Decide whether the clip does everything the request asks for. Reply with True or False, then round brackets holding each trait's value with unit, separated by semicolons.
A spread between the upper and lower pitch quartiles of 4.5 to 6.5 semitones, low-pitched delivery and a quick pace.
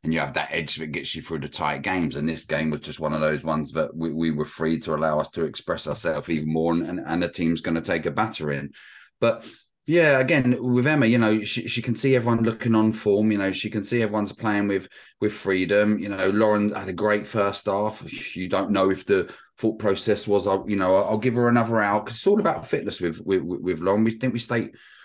True (5.5 semitones; 100 Hz; 250 wpm)